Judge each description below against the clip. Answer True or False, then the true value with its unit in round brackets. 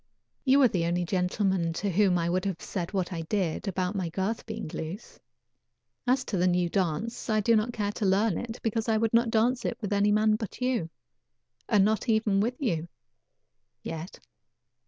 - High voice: True (205 Hz)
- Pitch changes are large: False (3.8 semitones)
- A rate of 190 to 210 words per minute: True (195 wpm)